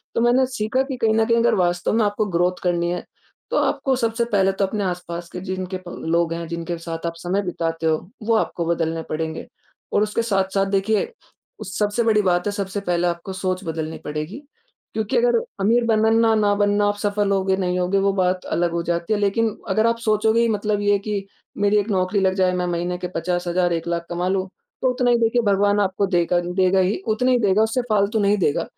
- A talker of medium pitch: No, high, 195 Hz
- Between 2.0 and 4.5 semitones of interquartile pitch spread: Yes, average, 3.5 semitones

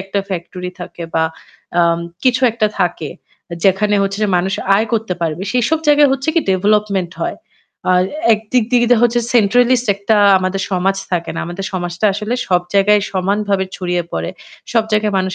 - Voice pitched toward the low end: No, high, 200 Hz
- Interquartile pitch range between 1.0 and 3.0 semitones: No, average, 3.4 semitones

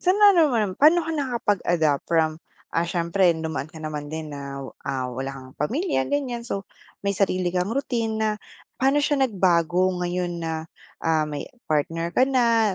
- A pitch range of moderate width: No, wide, 6.9 semitones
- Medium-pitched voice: Yes, medium, 180 Hz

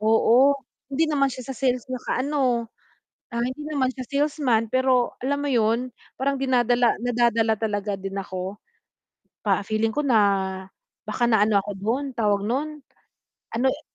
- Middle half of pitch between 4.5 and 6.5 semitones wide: No, average, 3.5 semitones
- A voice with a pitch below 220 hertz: No, high, 245 Hz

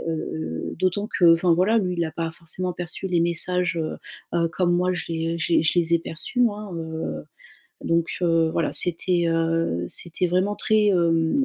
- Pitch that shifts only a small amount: Yes, narrow, 1.8 semitones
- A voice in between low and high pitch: Yes, medium, 170 Hz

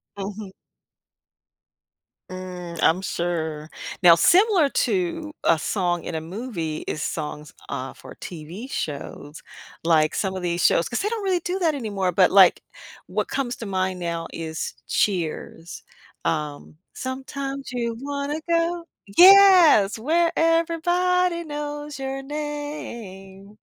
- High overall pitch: Yes, high, 220 Hz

